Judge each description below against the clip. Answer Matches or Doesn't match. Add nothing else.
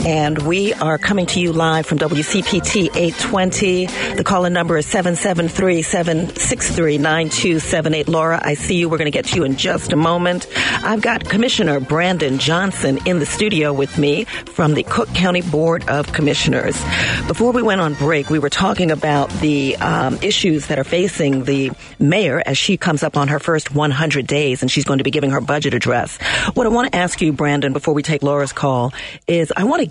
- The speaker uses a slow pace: Doesn't match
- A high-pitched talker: Doesn't match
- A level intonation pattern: Doesn't match